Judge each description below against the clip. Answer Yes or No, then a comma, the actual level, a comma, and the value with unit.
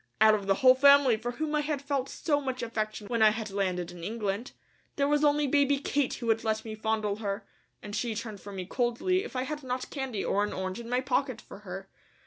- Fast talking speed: Yes, fast, 240 wpm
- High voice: Yes, high, 235 Hz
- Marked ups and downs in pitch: No, average, 4.8 semitones